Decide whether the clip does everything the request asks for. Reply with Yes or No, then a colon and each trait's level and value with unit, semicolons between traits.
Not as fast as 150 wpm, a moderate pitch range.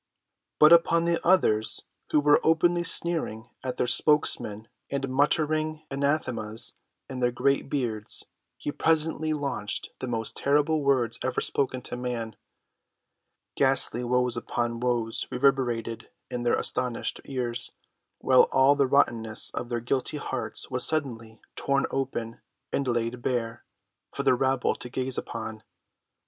Yes: slow, 135 wpm; average, 3.4 semitones